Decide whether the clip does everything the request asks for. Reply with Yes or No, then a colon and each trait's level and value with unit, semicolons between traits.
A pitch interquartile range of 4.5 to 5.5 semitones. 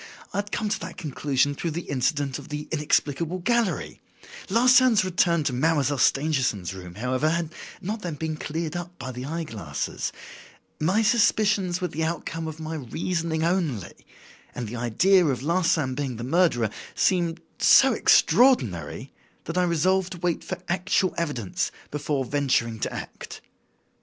Yes: average, 5.2 semitones